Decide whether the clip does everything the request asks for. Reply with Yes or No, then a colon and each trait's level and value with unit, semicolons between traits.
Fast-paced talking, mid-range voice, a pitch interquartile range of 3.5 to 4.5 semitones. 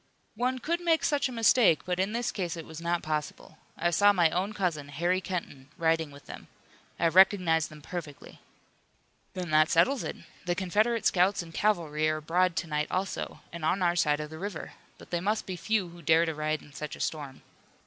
Yes: fast, 210 wpm; medium, 175 Hz; average, 3.8 semitones